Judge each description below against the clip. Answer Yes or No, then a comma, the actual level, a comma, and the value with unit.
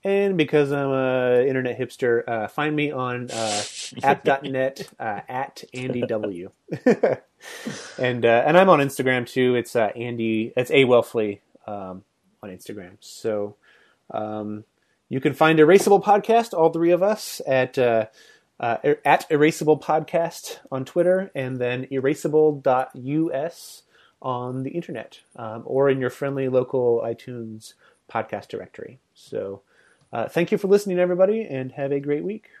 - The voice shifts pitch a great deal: No, average, 4.4 semitones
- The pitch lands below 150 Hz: Yes, low, 135 Hz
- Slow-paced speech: No, average, 145 wpm